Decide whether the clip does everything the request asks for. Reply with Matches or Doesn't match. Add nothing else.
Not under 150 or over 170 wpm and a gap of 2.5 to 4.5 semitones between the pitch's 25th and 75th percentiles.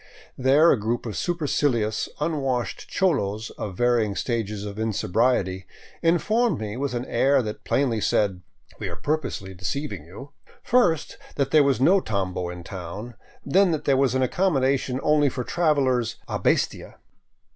Doesn't match